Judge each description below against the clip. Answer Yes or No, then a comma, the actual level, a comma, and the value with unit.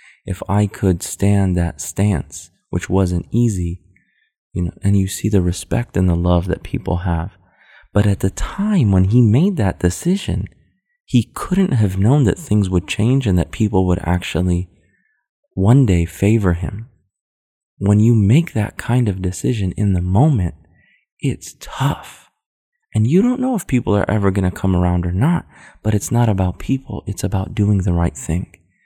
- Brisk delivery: No, average, 175 wpm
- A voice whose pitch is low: Yes, very low, 95 Hz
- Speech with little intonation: No, average, 3.8 semitones